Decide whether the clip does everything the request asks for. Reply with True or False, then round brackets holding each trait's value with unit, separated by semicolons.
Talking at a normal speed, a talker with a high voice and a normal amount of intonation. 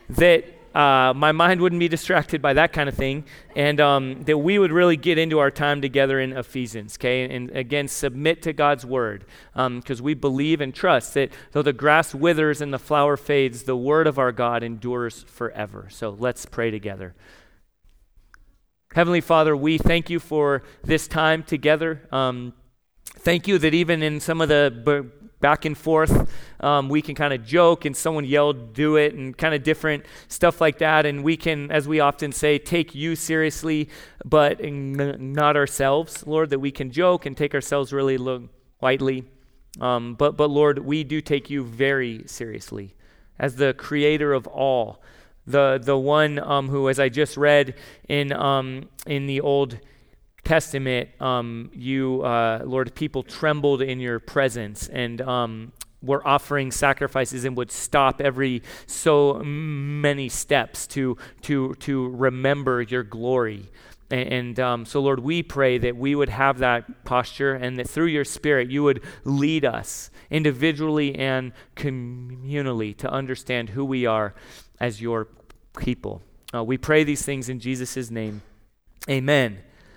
False (165 wpm; 140 Hz; 3.0 semitones)